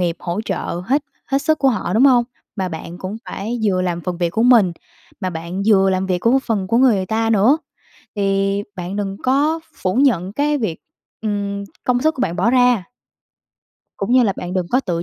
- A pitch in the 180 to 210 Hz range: Yes, high, 200 Hz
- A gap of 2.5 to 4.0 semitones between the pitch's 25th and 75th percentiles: No, average, 5.1 semitones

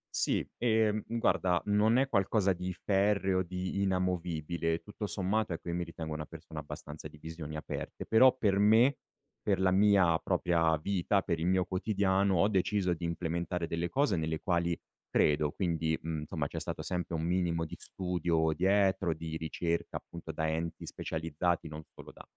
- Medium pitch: No, very low, 90 Hz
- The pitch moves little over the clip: No, average, 3.2 semitones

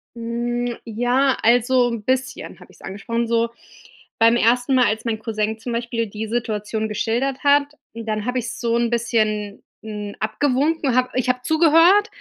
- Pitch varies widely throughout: No, narrow, 2.4 semitones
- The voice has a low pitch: No, high, 235 Hz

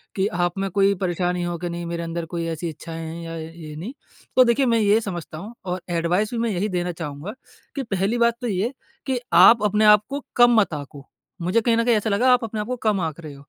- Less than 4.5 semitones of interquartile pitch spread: No, average, 4.8 semitones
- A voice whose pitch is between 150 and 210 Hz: Yes, high, 190 Hz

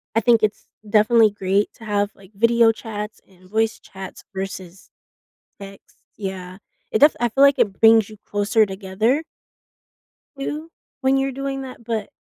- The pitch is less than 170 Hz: No, high, 215 Hz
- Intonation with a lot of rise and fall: No, average, 3.2 semitones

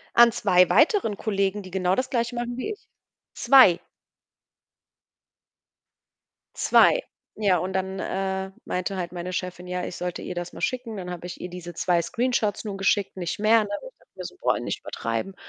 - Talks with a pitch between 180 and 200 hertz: Yes, high, 190 Hz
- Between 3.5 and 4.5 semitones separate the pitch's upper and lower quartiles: Yes, average, 3.8 semitones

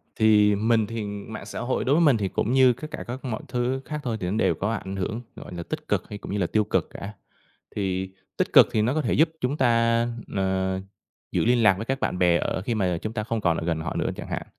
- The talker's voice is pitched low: Yes, low, 110 Hz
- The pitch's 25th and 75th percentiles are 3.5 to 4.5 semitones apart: Yes, average, 4.1 semitones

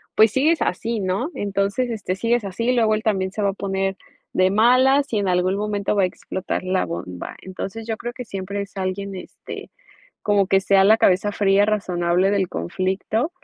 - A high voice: Yes, high, 200 Hz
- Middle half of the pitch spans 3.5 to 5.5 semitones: No, narrow, 2.6 semitones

